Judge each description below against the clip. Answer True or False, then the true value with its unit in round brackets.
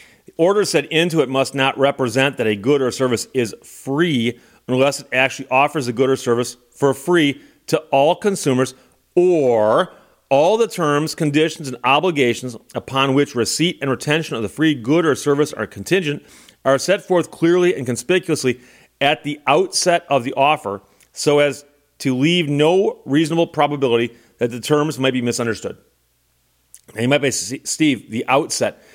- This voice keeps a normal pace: True (165 wpm)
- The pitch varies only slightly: False (4.0 semitones)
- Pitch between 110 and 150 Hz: True (140 Hz)